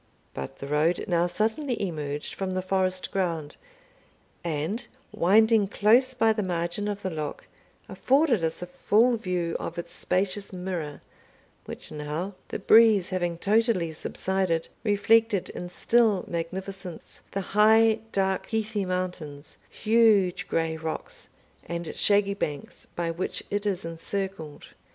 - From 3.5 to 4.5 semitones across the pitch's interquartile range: Yes, average, 3.8 semitones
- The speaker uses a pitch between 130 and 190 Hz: Yes, medium, 185 Hz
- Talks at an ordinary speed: No, slow, 130 wpm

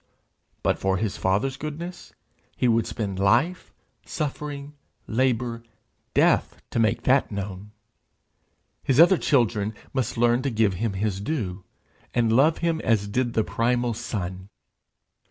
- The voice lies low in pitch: Yes, low, 115 Hz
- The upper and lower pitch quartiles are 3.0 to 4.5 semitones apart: No, average, 4.9 semitones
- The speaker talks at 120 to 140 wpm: Yes, slow, 135 wpm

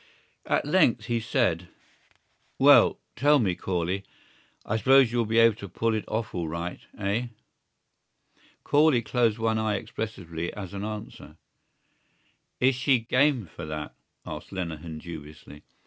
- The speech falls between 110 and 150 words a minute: Yes, slow, 135 wpm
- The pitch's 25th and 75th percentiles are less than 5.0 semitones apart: No, wide, 5.5 semitones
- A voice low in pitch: Yes, low, 110 Hz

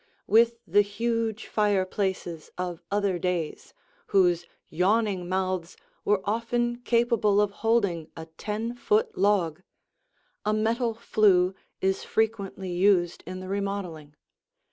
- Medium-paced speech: No, slow, 115 wpm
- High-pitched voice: Yes, high, 200 Hz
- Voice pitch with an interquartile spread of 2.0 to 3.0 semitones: No, average, 3.6 semitones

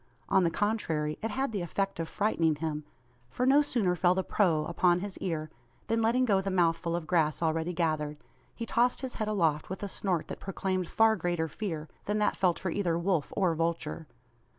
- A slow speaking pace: No, average, 200 wpm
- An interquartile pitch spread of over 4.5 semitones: No, average, 4.2 semitones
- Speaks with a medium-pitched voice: Yes, medium, 180 Hz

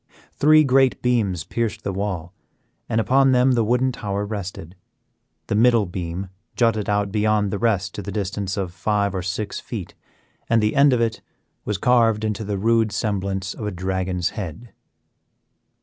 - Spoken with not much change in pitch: No, average, 3.2 semitones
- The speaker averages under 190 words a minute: Yes, average, 165 wpm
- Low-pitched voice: Yes, low, 105 Hz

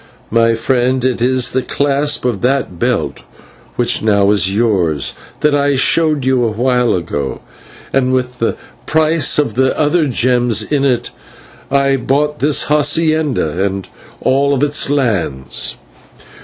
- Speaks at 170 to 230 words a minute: No, average, 140 wpm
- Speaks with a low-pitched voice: Yes, low, 130 Hz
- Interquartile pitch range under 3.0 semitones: No, average, 3.9 semitones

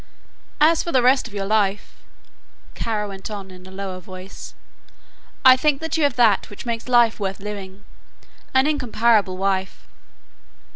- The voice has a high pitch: Yes, high, 210 Hz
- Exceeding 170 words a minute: No, average, 150 wpm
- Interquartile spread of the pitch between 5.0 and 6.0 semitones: No, average, 4.4 semitones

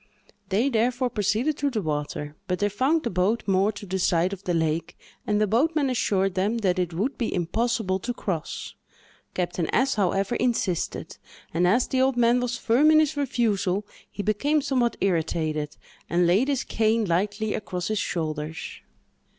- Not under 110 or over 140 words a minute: No, average, 175 wpm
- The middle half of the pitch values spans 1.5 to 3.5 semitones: No, average, 5.2 semitones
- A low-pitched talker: No, high, 205 Hz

